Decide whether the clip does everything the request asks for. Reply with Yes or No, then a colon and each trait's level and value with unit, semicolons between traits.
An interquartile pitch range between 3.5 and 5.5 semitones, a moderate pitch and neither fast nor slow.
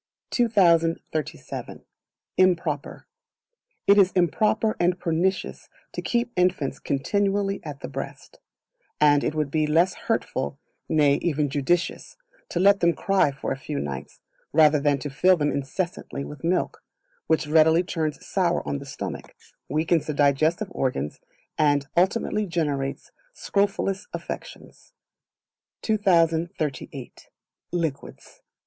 No: average, 4.3 semitones; medium, 160 Hz; slow, 120 wpm